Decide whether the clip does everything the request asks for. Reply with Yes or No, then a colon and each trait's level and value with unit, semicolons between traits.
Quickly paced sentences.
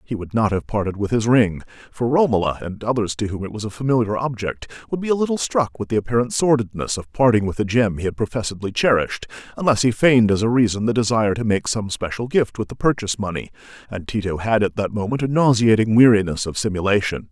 Yes: fast, 225 wpm